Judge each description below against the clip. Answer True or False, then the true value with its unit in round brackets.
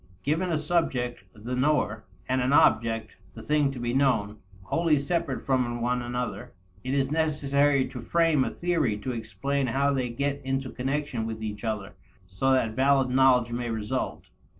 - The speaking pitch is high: False (130 Hz)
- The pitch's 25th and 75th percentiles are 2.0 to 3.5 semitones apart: True (3.2 semitones)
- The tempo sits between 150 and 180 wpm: True (170 wpm)